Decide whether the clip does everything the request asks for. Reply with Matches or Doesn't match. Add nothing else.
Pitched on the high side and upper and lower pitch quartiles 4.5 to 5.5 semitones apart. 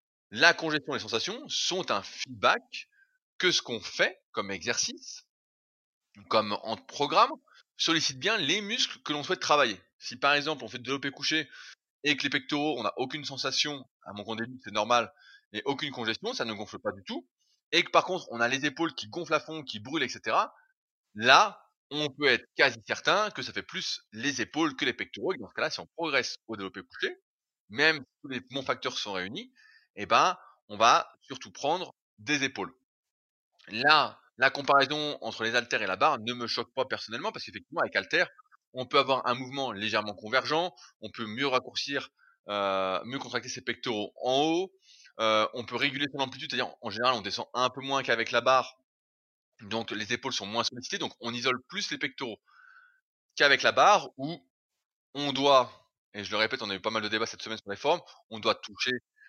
Doesn't match